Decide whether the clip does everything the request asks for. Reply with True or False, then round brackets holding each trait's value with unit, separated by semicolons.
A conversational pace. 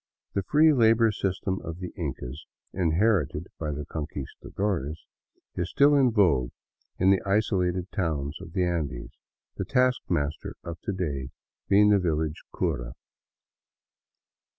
False (130 wpm)